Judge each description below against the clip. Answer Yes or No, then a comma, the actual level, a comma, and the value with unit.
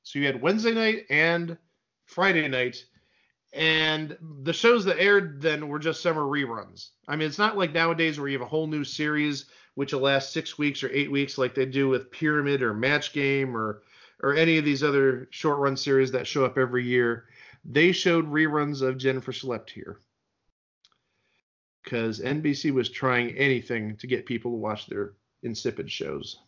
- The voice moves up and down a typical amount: Yes, average, 3.6 semitones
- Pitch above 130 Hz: Yes, medium, 140 Hz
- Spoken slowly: No, average, 185 wpm